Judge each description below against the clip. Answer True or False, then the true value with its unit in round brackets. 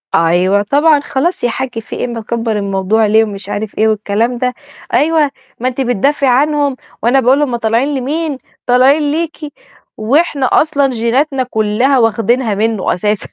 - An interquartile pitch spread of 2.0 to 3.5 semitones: False (4.3 semitones)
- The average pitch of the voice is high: True (245 Hz)